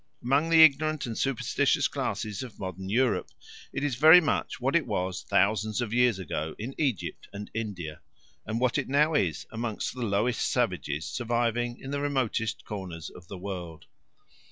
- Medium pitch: No, low, 115 Hz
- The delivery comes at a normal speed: Yes, average, 170 wpm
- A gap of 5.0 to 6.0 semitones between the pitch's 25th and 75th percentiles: Yes, wide, 5.5 semitones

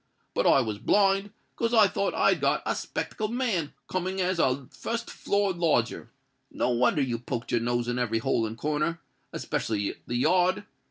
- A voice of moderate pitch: Yes, medium, 150 Hz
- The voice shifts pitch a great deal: Yes, wide, 8.2 semitones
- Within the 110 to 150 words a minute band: No, average, 170 wpm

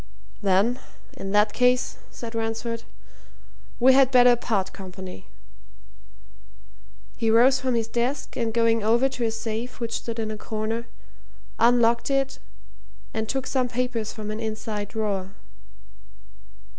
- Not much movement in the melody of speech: Yes, narrow, 2.2 semitones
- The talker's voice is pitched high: Yes, high, 230 Hz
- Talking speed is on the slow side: Yes, slow, 130 wpm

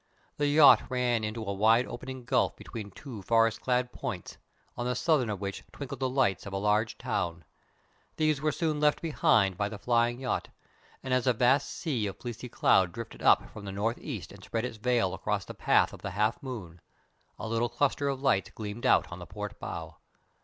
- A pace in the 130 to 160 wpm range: No, fast, 205 wpm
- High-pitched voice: No, low, 120 Hz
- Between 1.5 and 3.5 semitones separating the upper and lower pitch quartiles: No, average, 3.9 semitones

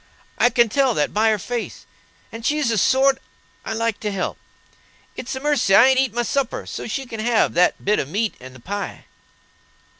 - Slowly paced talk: No, fast, 205 wpm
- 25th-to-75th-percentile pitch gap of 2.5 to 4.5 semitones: Yes, average, 4.0 semitones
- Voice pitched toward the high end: Yes, high, 230 Hz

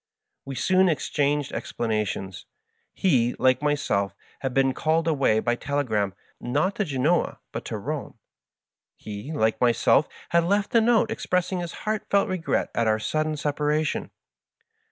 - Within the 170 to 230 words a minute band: No, average, 140 wpm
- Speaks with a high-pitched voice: No, medium, 145 Hz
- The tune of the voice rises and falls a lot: Yes, wide, 6.1 semitones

